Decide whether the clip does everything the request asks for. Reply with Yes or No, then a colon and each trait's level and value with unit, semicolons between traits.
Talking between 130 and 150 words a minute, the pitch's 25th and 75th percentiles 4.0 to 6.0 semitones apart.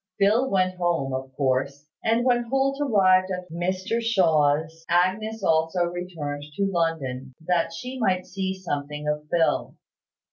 Yes: average, 140 wpm; average, 4.7 semitones